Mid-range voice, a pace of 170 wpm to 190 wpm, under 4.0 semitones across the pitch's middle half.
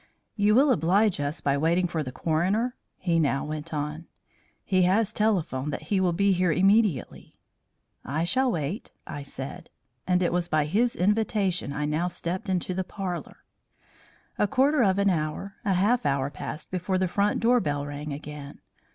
No: medium, 180 Hz; average, 175 wpm; average, 5.0 semitones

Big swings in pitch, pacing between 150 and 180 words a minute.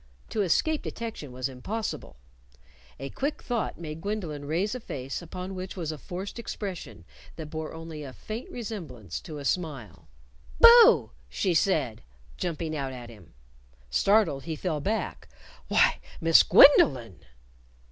No: wide, 6.8 semitones; average, 140 wpm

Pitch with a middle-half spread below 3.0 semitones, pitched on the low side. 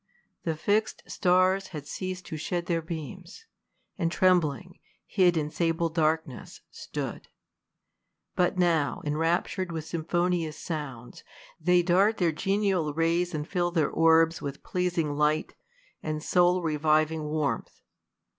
No: narrow, 2.6 semitones; medium, 165 Hz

